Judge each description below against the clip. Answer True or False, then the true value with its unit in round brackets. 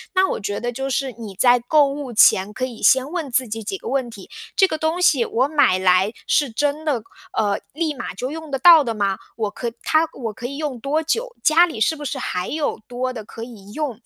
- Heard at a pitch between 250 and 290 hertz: True (255 Hz)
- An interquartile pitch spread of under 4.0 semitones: False (5.2 semitones)